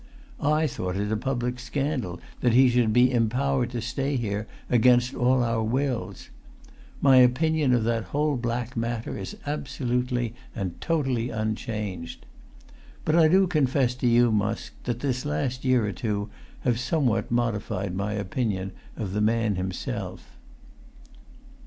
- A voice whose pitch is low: Yes, low, 120 Hz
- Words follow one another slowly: No, average, 145 wpm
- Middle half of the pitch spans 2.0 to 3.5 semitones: Yes, average, 3.1 semitones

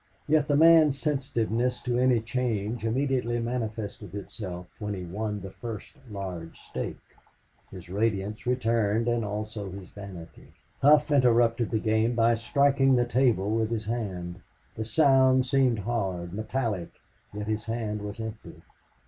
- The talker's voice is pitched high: No, low, 115 Hz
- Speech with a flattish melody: No, average, 3.3 semitones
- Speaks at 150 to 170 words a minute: No, average, 140 wpm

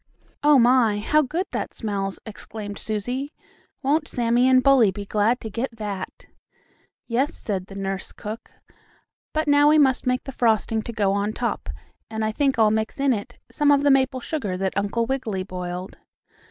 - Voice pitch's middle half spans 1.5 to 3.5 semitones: No, average, 4.7 semitones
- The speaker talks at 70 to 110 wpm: No, average, 180 wpm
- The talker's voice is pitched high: Yes, high, 230 Hz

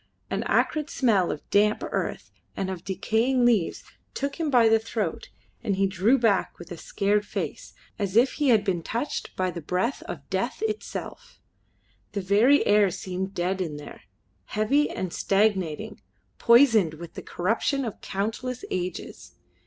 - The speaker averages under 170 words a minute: Yes, average, 160 wpm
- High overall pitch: Yes, high, 205 Hz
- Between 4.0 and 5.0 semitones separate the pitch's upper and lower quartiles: Yes, average, 4.4 semitones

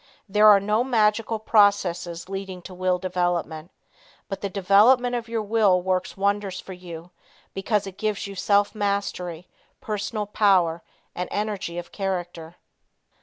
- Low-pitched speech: No, high, 195 Hz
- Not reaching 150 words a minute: Yes, average, 140 wpm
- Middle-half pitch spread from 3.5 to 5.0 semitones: No, average, 2.7 semitones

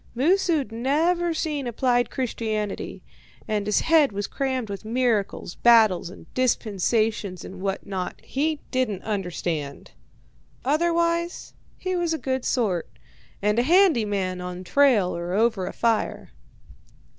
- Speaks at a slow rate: Yes, slow, 130 wpm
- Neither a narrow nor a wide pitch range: No, wide, 6.2 semitones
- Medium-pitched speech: No, high, 230 Hz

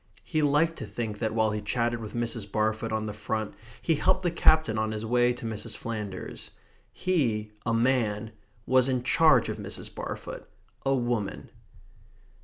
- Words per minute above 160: Yes, average, 170 wpm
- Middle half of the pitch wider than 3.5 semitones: No, average, 3.2 semitones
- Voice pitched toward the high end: No, low, 115 Hz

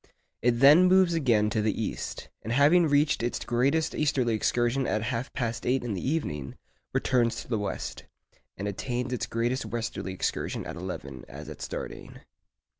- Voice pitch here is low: Yes, low, 120 Hz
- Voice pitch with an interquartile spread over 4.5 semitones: No, average, 4.0 semitones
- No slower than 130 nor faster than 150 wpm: No, average, 170 wpm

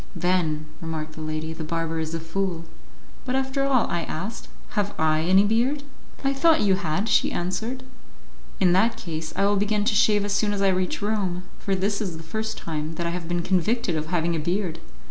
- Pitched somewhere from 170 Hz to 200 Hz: Yes, medium, 185 Hz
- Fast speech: Yes, fast, 210 wpm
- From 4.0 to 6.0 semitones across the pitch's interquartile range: Yes, average, 4.5 semitones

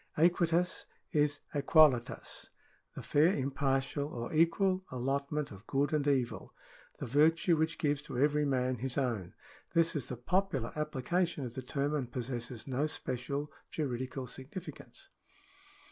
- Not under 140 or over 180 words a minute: Yes, average, 145 wpm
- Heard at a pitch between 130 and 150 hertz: Yes, medium, 140 Hz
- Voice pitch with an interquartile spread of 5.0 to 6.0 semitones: No, average, 3.4 semitones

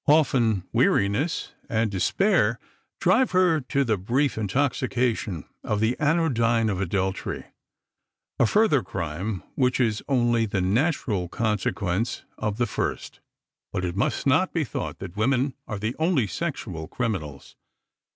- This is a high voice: No, low, 115 Hz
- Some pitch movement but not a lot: No, wide, 5.8 semitones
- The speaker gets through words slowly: Yes, slow, 130 wpm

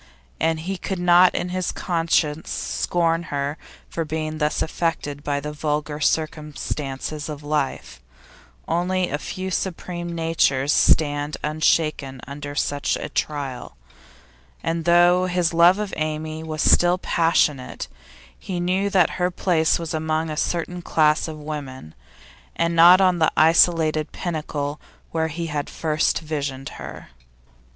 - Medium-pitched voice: Yes, medium, 160 Hz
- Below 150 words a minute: Yes, average, 140 wpm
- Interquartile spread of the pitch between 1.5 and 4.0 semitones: Yes, narrow, 2.5 semitones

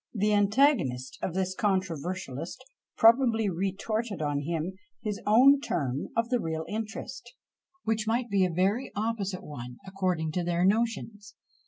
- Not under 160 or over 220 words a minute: No, average, 145 wpm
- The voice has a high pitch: Yes, high, 195 Hz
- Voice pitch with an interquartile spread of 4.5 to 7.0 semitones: Yes, average, 4.8 semitones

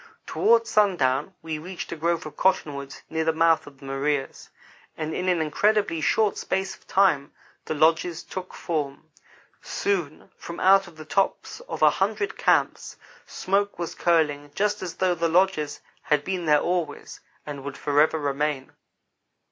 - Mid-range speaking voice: Yes, medium, 160 Hz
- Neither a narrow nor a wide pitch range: Yes, average, 4.1 semitones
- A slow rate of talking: No, average, 155 wpm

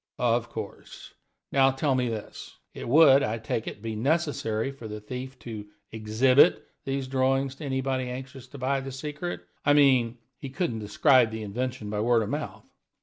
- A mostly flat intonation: No, average, 3.3 semitones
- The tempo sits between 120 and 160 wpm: No, average, 175 wpm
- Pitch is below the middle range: Yes, low, 130 Hz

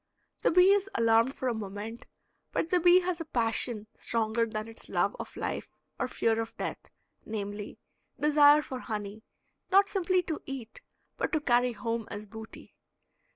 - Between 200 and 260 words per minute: No, average, 165 wpm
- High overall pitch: Yes, high, 235 Hz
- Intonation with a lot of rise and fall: Yes, wide, 5.9 semitones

